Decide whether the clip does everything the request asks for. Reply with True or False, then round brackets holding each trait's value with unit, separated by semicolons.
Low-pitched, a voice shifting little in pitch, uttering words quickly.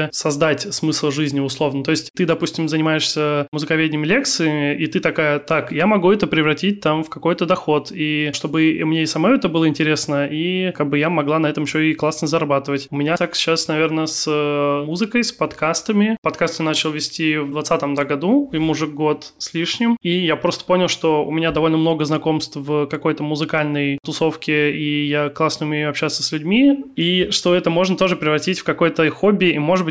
False (155 Hz; 2.0 semitones; 190 wpm)